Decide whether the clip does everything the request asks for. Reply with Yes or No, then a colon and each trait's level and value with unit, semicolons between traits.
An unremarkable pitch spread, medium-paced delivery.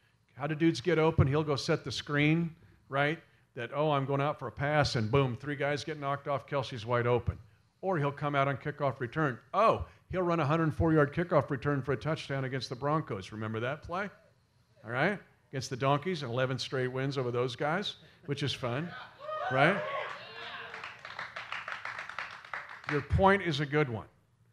Yes: average, 3.6 semitones; average, 185 wpm